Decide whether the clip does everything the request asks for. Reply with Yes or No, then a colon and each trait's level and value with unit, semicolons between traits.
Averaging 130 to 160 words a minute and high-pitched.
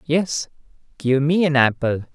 No: average, 140 wpm; medium, 145 Hz